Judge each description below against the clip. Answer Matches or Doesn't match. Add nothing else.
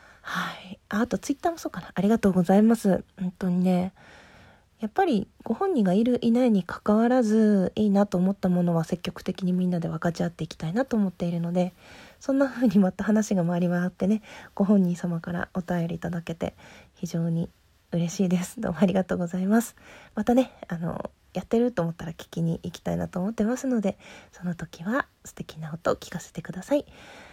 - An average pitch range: Matches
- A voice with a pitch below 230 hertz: Matches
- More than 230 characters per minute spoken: Matches